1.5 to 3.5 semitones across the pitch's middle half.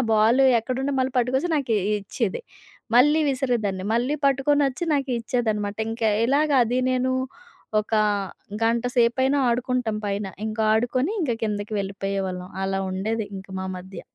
No: average, 4.0 semitones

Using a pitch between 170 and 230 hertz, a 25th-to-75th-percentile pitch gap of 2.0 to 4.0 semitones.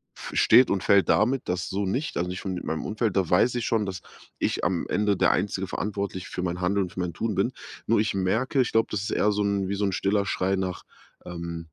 No: low, 100 Hz; narrow, 2.5 semitones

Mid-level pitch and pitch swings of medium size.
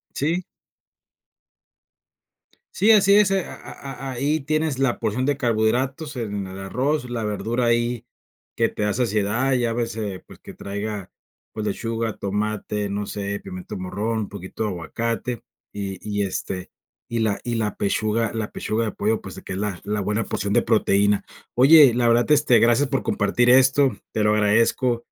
No: low, 115 Hz; average, 3.5 semitones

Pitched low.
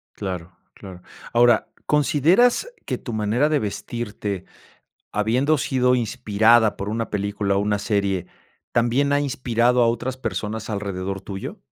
Yes: low, 110 Hz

